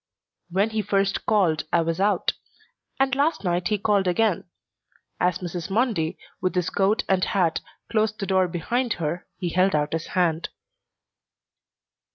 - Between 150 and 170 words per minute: Yes, average, 155 wpm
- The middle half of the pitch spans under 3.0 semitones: No, average, 3.4 semitones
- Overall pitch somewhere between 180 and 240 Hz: Yes, high, 190 Hz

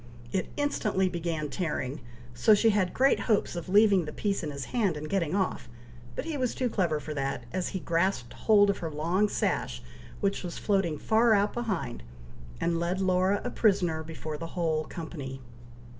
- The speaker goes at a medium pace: Yes, average, 185 wpm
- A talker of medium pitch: Yes, medium, 180 Hz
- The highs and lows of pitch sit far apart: No, average, 4.5 semitones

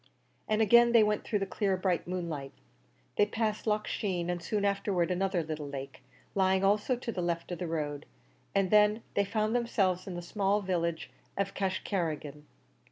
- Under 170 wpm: No, average, 175 wpm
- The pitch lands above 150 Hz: Yes, high, 190 Hz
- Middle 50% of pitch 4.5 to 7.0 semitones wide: No, average, 3.6 semitones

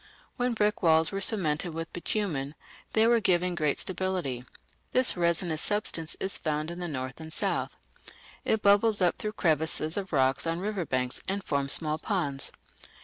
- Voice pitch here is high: No, medium, 170 Hz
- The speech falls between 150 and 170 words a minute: Yes, average, 165 wpm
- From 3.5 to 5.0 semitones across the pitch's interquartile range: Yes, average, 4.6 semitones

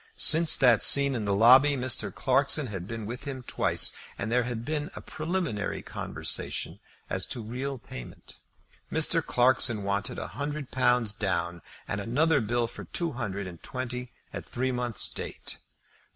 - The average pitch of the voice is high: No, low, 125 Hz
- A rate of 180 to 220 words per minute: No, average, 160 wpm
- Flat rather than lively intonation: No, average, 4.2 semitones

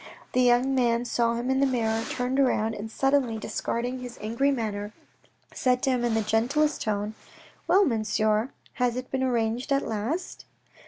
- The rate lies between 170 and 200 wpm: Yes, average, 175 wpm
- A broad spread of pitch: No, average, 2.9 semitones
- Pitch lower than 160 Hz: No, high, 240 Hz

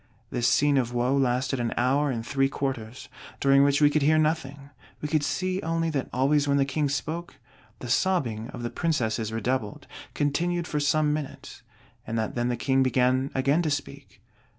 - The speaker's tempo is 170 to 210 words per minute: Yes, average, 185 wpm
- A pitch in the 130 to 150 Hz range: Yes, medium, 140 Hz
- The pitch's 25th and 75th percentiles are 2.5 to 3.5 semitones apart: Yes, average, 3.1 semitones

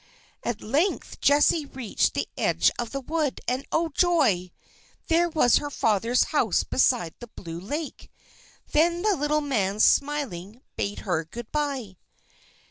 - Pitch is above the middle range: Yes, very high, 265 Hz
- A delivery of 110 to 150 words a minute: Yes, average, 140 wpm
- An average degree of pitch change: No, wide, 6.1 semitones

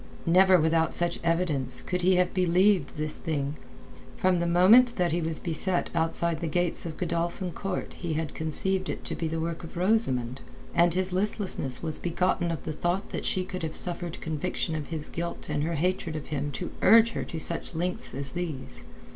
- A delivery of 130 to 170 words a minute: No, average, 195 wpm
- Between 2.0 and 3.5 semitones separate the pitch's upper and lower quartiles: Yes, narrow, 2.4 semitones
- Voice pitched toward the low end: No, medium, 170 Hz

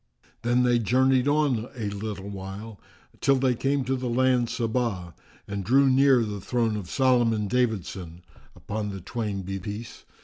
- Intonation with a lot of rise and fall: No, average, 4.0 semitones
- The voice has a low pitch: Yes, low, 115 Hz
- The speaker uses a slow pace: No, average, 165 wpm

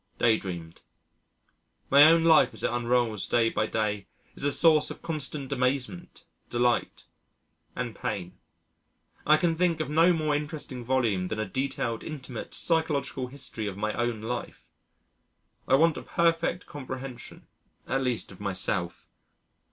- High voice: No, low, 130 Hz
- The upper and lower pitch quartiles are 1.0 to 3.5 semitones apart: No, wide, 5.5 semitones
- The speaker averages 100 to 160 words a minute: Yes, average, 145 wpm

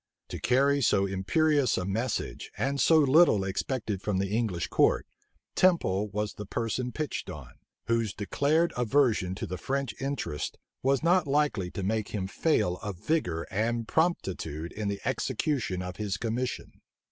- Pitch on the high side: No, low, 110 Hz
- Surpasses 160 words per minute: No, average, 155 wpm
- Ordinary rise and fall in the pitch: No, wide, 6.2 semitones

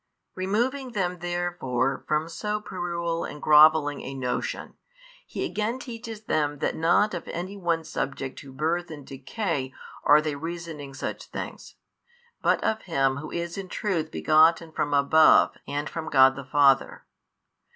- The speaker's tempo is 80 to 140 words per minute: No, average, 150 wpm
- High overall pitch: No, medium, 160 Hz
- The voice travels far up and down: No, average, 3.8 semitones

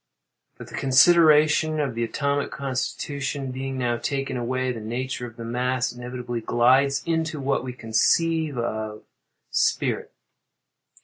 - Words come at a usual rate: No, slow, 130 wpm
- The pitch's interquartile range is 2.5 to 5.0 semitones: Yes, average, 2.8 semitones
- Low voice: Yes, low, 130 Hz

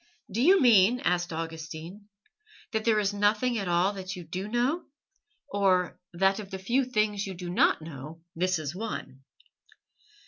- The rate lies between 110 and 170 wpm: Yes, average, 165 wpm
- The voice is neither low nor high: No, high, 195 Hz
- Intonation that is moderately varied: Yes, average, 3.7 semitones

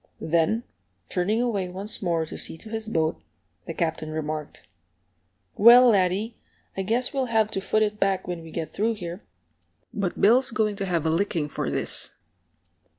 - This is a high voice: Yes, high, 195 Hz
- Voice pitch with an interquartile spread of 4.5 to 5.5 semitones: Yes, average, 4.8 semitones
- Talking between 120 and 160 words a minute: No, average, 170 wpm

